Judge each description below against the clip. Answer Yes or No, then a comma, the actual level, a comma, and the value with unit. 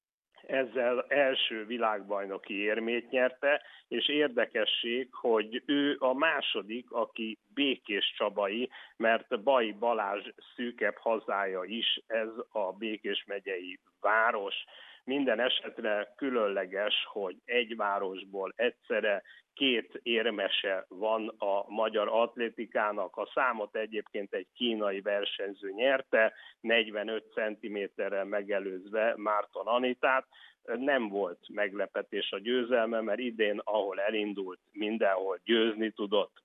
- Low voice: Yes, low, 110 Hz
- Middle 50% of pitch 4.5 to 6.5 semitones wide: No, average, 2.7 semitones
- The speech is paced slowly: Yes, slow, 100 wpm